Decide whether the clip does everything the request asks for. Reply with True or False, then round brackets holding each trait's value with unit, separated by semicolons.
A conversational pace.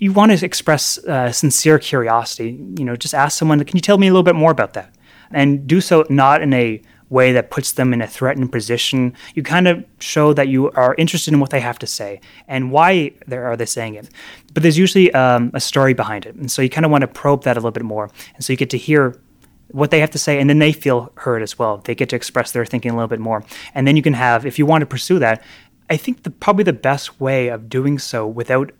False (265 wpm)